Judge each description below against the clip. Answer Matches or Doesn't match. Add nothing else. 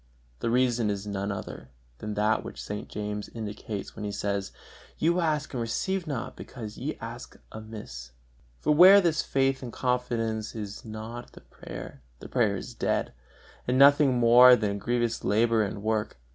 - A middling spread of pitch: Matches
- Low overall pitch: Matches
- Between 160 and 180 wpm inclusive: Matches